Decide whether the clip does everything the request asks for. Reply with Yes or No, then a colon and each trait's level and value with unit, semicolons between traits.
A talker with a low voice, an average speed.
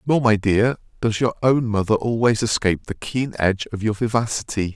Yes: low, 110 Hz; average, 190 wpm